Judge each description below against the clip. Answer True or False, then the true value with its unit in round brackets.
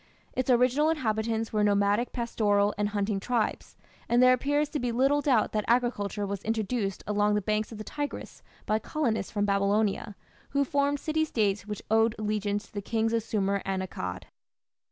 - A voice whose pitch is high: True (220 Hz)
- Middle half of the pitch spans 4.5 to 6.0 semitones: False (3.4 semitones)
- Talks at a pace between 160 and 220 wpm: True (175 wpm)